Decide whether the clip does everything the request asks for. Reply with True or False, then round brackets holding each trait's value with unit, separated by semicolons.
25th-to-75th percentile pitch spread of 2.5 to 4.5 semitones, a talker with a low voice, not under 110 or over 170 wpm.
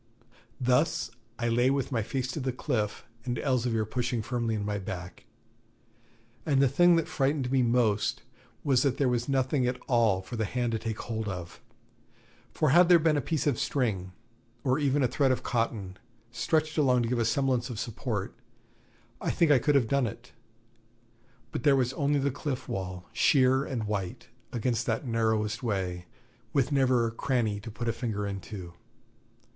False (3.6 semitones; 120 Hz; 180 wpm)